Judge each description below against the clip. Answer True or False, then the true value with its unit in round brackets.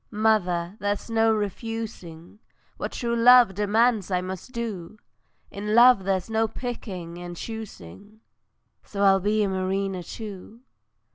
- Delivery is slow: True (130 wpm)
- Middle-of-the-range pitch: False (205 Hz)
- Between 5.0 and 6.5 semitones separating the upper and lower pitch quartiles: False (3.2 semitones)